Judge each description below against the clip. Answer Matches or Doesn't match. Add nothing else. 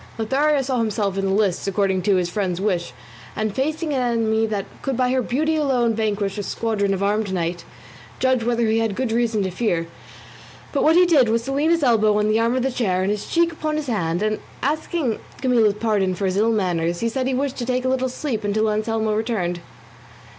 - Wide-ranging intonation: Doesn't match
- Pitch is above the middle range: Matches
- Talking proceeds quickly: Matches